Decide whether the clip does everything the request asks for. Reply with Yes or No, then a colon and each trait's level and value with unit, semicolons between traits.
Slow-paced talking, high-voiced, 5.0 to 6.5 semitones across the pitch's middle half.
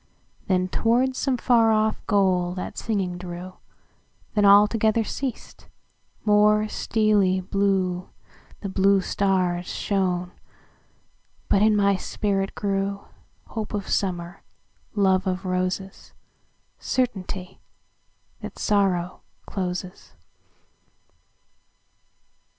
No: slow, 80 wpm; high, 195 Hz; narrow, 2.4 semitones